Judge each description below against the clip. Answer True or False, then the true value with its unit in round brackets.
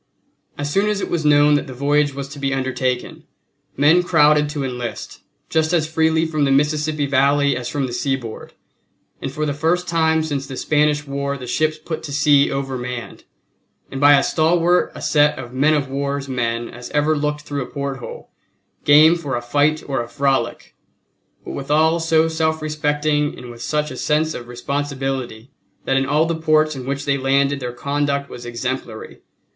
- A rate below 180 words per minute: False (185 wpm)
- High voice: False (145 Hz)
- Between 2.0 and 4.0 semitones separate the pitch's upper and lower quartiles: True (2.4 semitones)